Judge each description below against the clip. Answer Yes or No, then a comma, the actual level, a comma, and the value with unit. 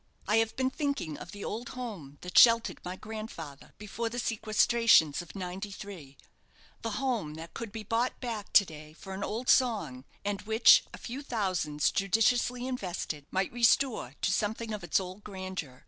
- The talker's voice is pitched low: No, high, 205 Hz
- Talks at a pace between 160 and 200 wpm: Yes, average, 170 wpm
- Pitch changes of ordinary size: Yes, average, 4.6 semitones